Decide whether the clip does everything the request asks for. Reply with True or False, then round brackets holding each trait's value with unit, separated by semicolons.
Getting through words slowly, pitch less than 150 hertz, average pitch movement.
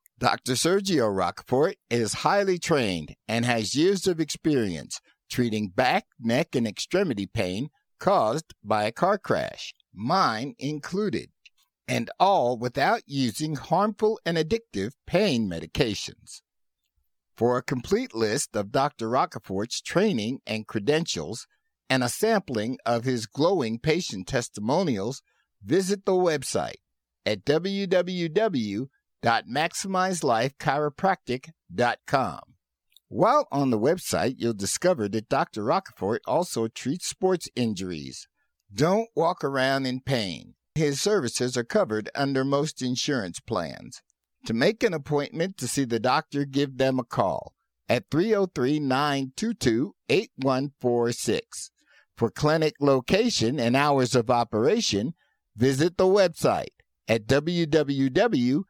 False (115 wpm; 140 Hz; 6.3 semitones)